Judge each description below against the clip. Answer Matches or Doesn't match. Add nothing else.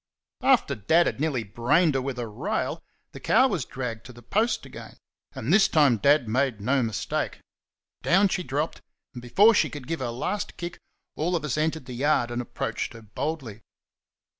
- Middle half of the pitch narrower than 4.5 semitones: Doesn't match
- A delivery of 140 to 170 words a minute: Doesn't match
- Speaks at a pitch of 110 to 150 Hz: Matches